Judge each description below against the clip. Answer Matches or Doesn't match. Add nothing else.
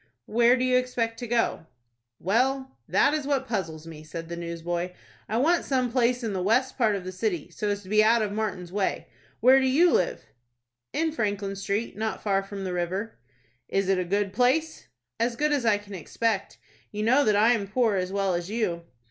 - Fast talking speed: Matches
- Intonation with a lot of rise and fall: Doesn't match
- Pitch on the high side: Matches